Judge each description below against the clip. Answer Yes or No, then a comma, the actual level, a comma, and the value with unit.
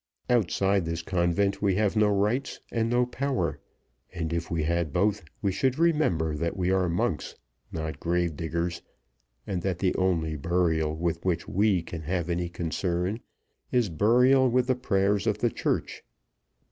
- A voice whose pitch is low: Yes, very low, 90 Hz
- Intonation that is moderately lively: Yes, average, 4.0 semitones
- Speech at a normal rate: Yes, average, 160 wpm